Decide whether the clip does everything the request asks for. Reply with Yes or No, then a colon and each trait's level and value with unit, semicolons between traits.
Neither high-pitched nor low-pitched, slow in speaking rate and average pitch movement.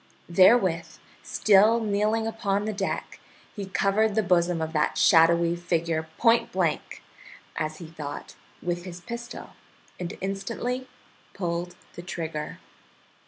Yes: medium, 180 Hz; slow, 120 wpm; average, 4.0 semitones